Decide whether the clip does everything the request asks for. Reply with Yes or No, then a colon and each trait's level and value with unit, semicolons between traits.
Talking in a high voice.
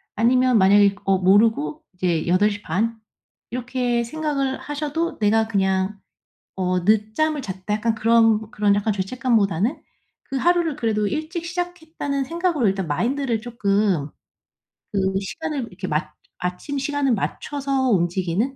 Yes: high, 225 Hz